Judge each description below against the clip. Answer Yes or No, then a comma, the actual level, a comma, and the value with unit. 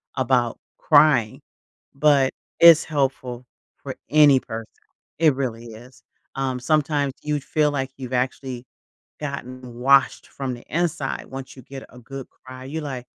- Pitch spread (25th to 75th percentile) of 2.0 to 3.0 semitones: Yes, narrow, 2.4 semitones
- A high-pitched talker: No, low, 135 Hz